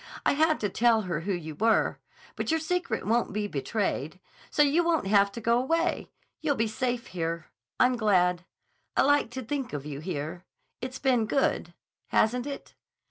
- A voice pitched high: Yes, high, 225 Hz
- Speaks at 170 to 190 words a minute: Yes, average, 175 wpm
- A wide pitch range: Yes, wide, 6.6 semitones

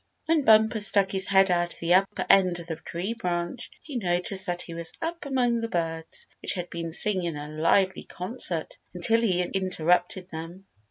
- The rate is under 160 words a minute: No, average, 195 wpm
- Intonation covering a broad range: No, average, 3.7 semitones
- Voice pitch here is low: No, medium, 185 Hz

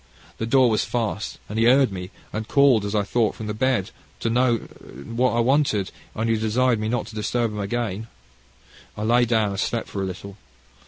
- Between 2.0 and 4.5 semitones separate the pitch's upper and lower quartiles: Yes, narrow, 2.5 semitones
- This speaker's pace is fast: Yes, fast, 210 wpm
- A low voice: Yes, low, 110 Hz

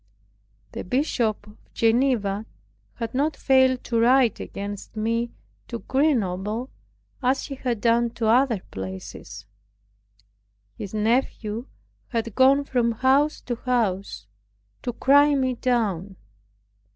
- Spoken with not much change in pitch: No, average, 3.7 semitones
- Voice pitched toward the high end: Yes, high, 235 Hz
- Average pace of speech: No, slow, 115 wpm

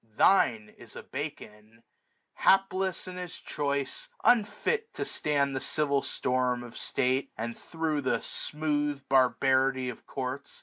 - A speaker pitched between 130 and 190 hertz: Yes, medium, 140 Hz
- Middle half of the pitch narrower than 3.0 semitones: No, average, 3.9 semitones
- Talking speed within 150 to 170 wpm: No, slow, 135 wpm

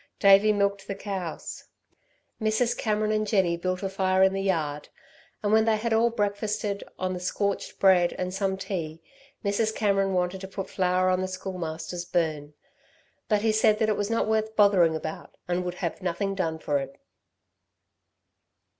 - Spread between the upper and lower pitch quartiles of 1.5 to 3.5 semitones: Yes, average, 2.8 semitones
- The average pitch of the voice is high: Yes, high, 195 Hz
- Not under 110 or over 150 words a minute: No, average, 170 wpm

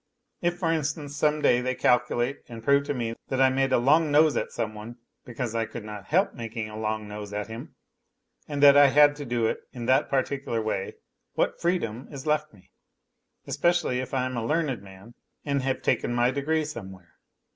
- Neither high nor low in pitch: No, low, 130 Hz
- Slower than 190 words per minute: No, fast, 205 wpm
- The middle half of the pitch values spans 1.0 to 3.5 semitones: No, average, 4.3 semitones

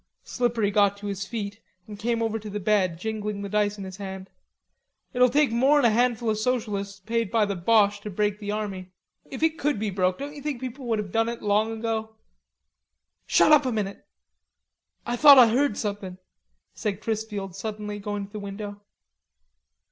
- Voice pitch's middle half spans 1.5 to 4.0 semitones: Yes, narrow, 2.5 semitones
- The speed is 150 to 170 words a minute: No, average, 190 wpm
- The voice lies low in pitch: No, high, 210 Hz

